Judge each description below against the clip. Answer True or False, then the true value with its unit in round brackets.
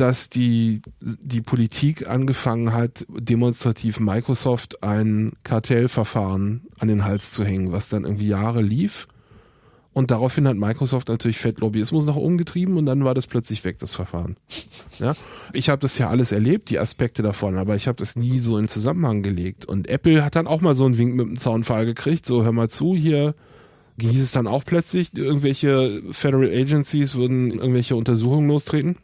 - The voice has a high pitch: False (125 Hz)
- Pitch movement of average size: True (3.8 semitones)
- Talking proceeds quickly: False (180 wpm)